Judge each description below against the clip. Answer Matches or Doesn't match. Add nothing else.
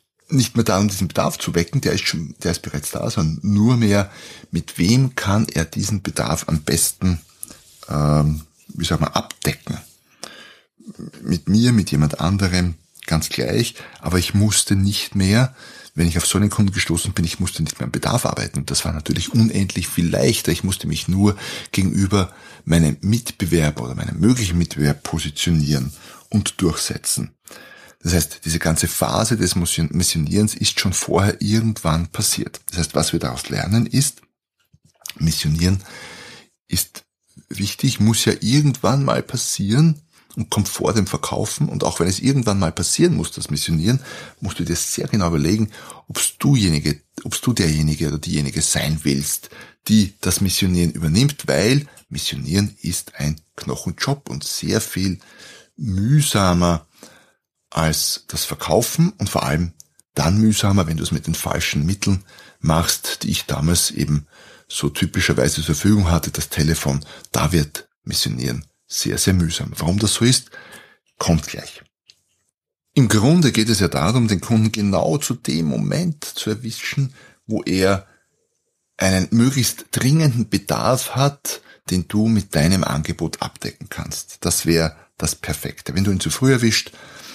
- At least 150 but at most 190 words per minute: Matches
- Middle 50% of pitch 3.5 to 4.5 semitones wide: Doesn't match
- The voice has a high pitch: Doesn't match